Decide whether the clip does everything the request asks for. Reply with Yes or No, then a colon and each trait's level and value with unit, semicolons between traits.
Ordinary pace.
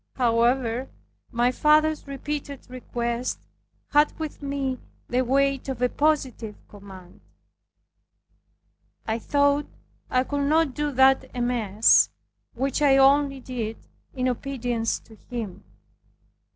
No: slow, 110 wpm